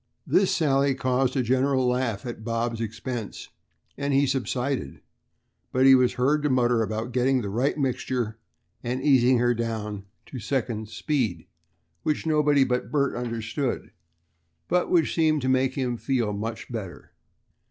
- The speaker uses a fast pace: No, average, 145 wpm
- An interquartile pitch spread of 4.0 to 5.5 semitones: No, average, 2.8 semitones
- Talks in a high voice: No, low, 125 Hz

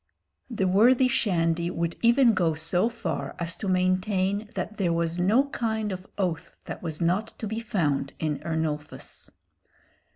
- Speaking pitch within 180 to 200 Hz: Yes, medium, 185 Hz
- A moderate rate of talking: Yes, average, 155 wpm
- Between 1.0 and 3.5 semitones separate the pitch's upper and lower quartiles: No, average, 4.6 semitones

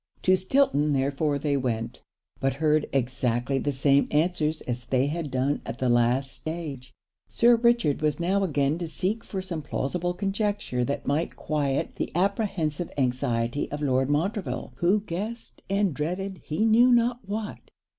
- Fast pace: No, average, 155 wpm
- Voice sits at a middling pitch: Yes, medium, 150 Hz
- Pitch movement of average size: No, wide, 6.1 semitones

